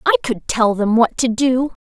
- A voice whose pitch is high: Yes, very high, 255 Hz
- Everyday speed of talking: No, fast, 230 wpm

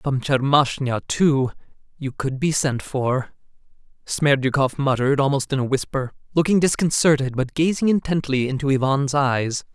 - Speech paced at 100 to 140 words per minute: Yes, slow, 135 wpm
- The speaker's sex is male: Yes, male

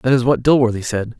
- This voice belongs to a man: Yes, male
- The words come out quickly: Yes, fast, 250 wpm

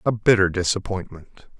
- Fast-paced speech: No, slow, 115 wpm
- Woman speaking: No, male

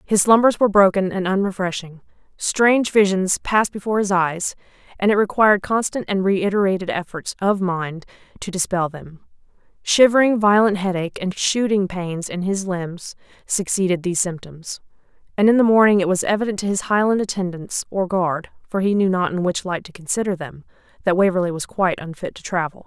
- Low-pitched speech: No, high, 190 Hz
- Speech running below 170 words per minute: No, average, 175 wpm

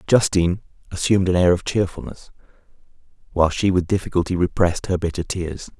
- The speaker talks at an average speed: Yes, average, 145 wpm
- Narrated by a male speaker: Yes, male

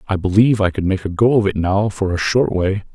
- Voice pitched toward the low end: Yes, low, 100 Hz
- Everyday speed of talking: No, fast, 285 wpm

